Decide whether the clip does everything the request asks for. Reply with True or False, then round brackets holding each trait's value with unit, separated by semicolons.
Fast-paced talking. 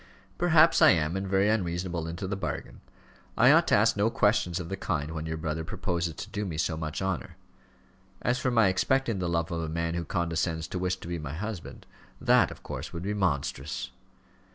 True (210 wpm)